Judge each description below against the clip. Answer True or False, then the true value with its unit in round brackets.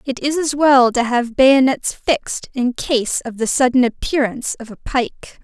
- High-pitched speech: True (255 Hz)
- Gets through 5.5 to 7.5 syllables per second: False (4.7 syllables/s)